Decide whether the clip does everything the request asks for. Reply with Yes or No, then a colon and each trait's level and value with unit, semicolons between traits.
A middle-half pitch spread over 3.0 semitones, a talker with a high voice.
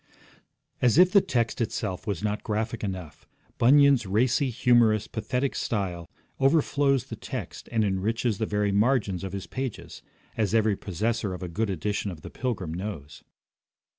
No: average, 4.2 semitones; low, 110 Hz